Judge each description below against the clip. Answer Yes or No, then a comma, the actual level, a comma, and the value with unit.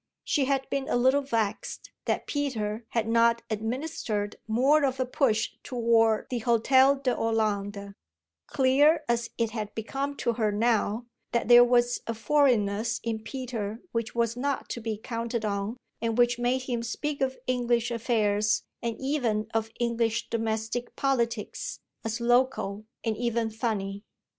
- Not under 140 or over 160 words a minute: Yes, average, 150 wpm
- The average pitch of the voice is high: Yes, high, 235 Hz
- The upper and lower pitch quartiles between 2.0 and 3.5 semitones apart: Yes, narrow, 2.5 semitones